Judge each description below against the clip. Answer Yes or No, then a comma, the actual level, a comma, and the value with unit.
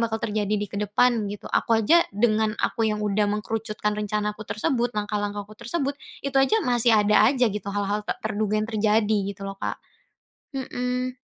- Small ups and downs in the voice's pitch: Yes, narrow, 2.0 semitones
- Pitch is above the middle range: Yes, high, 215 Hz